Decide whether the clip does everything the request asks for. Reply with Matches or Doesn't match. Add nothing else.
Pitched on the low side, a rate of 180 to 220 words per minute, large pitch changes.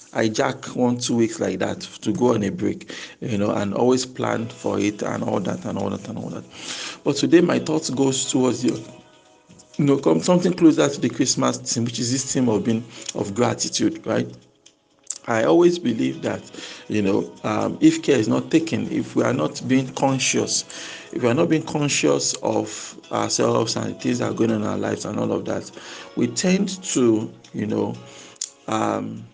Matches